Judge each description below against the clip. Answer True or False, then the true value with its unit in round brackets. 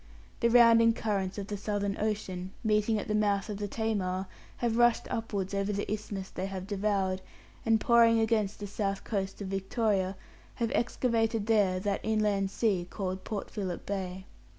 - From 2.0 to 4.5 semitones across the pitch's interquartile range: True (2.4 semitones)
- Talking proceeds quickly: False (170 wpm)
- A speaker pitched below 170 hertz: False (205 Hz)